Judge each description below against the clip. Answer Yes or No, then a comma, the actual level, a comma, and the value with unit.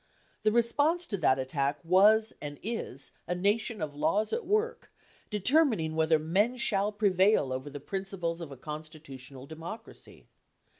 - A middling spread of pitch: No, wide, 6.3 semitones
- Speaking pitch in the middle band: Yes, medium, 180 Hz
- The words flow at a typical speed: Yes, average, 150 wpm